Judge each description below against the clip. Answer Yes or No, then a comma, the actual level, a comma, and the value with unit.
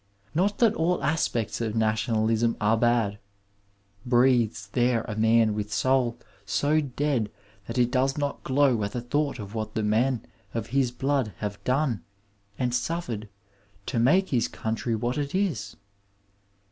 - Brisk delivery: No, average, 150 wpm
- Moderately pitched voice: No, low, 120 Hz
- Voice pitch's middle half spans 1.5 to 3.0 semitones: No, average, 3.7 semitones